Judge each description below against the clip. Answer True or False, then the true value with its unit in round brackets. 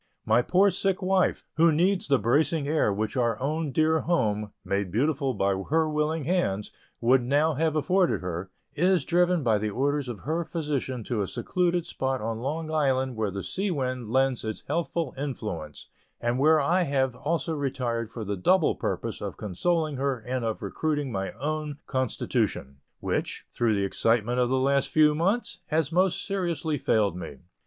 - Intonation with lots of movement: True (5.8 semitones)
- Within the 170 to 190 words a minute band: True (175 wpm)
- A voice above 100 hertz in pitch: True (140 Hz)